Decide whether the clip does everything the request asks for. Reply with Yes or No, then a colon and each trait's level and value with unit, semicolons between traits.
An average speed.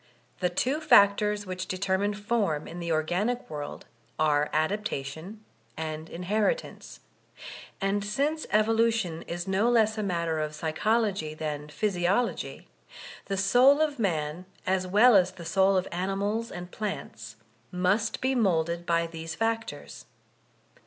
No: slow, 130 wpm